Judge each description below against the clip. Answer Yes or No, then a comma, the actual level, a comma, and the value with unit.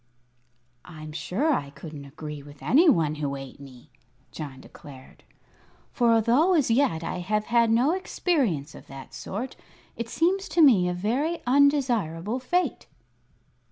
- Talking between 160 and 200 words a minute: No, average, 145 wpm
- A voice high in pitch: Yes, high, 215 Hz